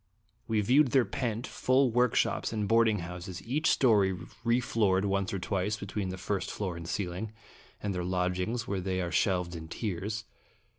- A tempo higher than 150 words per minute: Yes, average, 165 wpm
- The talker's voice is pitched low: Yes, low, 100 Hz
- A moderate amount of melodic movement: Yes, average, 3.7 semitones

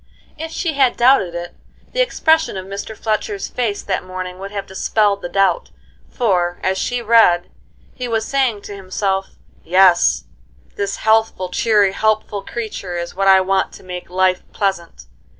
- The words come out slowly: No, average, 160 wpm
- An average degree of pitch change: Yes, average, 3.4 semitones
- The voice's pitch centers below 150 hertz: No, high, 200 Hz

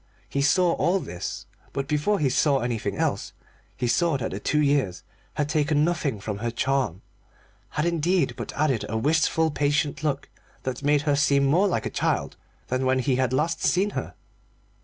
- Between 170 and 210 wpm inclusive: Yes, average, 180 wpm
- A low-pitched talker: No, medium, 145 Hz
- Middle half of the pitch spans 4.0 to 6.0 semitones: No, average, 3.2 semitones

